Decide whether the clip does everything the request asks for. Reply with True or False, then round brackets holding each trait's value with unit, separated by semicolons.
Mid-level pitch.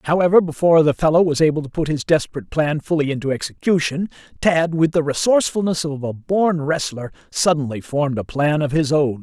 True (155 Hz)